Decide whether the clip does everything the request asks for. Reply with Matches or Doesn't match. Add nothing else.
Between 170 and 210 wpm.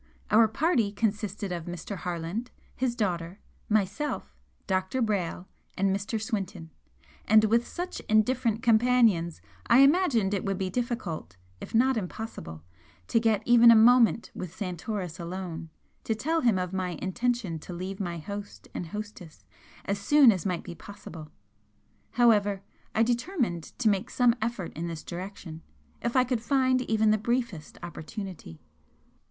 Doesn't match